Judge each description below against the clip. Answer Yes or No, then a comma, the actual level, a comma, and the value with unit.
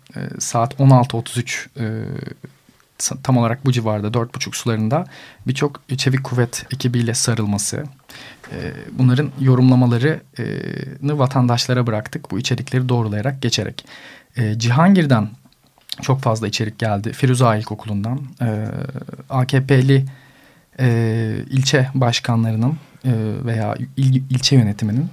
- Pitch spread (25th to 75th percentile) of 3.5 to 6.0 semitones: No, average, 2.7 semitones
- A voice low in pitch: Yes, low, 125 Hz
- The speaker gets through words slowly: Yes, slow, 85 wpm